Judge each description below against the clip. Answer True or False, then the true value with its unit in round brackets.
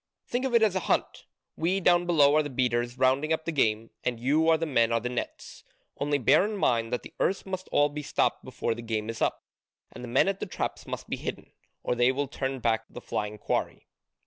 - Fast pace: True (240 wpm)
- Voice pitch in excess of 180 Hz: False (135 Hz)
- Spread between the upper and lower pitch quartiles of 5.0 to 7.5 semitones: True (5.6 semitones)